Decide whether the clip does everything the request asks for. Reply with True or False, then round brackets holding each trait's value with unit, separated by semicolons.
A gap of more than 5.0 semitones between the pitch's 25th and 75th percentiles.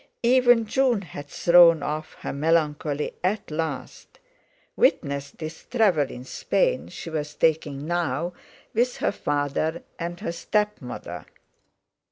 True (5.4 semitones)